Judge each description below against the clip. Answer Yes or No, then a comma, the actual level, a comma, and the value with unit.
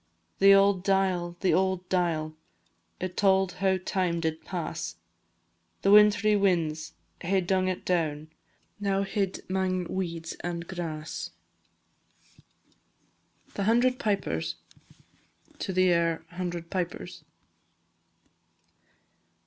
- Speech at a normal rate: No, slow, 95 wpm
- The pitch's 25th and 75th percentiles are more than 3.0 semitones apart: No, narrow, 2.4 semitones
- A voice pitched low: No, medium, 185 Hz